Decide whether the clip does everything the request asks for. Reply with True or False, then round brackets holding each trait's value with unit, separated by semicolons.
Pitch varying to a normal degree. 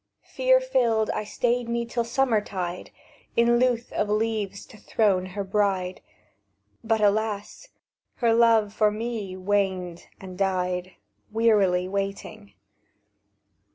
True (3.3 semitones)